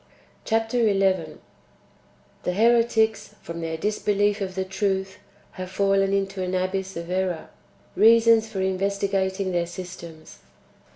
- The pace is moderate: No, slow, 130 wpm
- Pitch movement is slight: Yes, narrow, 2.1 semitones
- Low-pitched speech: No, high, 195 Hz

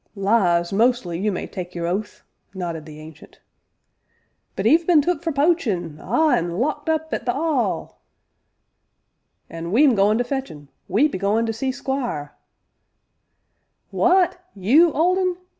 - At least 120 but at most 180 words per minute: Yes, average, 160 wpm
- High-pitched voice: Yes, high, 230 Hz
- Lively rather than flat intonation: Yes, wide, 9.0 semitones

